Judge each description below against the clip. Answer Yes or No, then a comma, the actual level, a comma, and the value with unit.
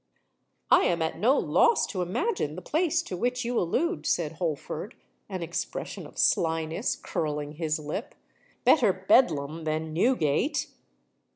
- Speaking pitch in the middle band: Yes, medium, 175 Hz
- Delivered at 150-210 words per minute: No, slow, 135 wpm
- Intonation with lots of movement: Yes, wide, 7.9 semitones